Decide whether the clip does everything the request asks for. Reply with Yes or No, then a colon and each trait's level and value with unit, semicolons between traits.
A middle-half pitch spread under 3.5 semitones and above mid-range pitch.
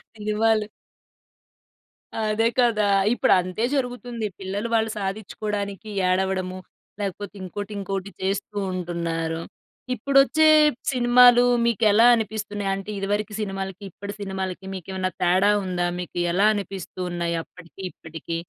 Yes: average, 2.8 semitones; high, 200 Hz